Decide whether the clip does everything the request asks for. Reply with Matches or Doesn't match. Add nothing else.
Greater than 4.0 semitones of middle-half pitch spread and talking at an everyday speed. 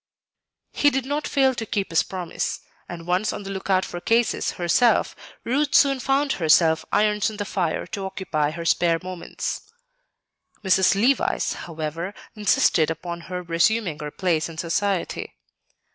Matches